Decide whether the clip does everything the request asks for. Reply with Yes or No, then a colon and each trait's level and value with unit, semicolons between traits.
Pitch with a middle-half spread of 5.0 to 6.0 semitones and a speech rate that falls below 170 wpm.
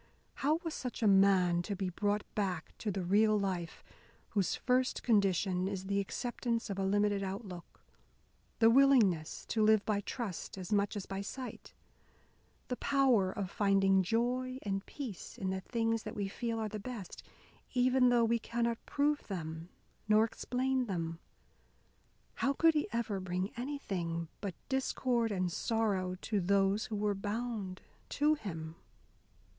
No: average, 3.8 semitones; average, 155 wpm